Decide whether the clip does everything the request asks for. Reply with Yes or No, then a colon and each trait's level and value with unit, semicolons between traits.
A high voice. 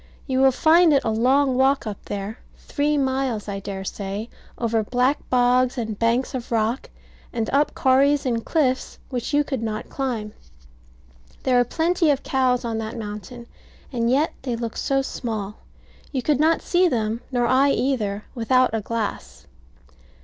Yes: high, 245 Hz